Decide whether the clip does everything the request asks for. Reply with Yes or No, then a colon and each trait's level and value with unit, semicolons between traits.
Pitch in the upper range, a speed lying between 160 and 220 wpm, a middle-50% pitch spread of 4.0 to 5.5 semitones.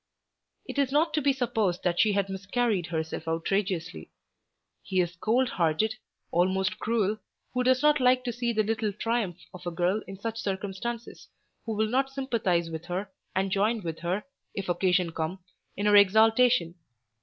Yes: high, 205 Hz; average, 170 wpm; average, 4.7 semitones